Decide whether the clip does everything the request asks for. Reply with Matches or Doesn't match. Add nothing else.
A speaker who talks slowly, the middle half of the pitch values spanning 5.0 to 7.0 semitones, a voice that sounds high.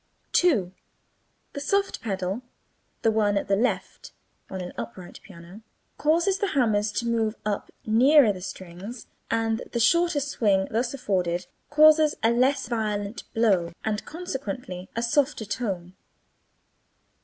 Matches